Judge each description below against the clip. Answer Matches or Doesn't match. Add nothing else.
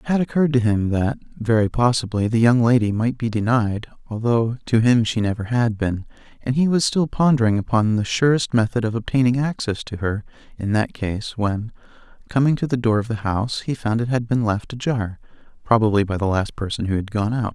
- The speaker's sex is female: Doesn't match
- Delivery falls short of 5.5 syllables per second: Doesn't match